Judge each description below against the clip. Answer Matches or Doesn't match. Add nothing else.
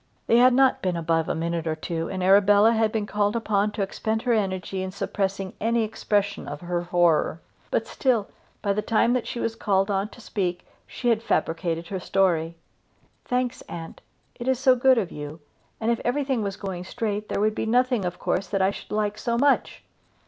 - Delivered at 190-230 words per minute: Matches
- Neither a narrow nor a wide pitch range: Matches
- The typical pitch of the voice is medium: Doesn't match